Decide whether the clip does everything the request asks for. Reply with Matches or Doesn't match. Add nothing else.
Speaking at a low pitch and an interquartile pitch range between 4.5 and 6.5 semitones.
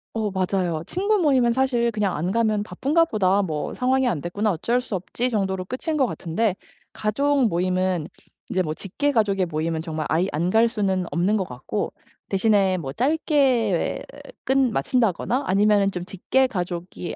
Doesn't match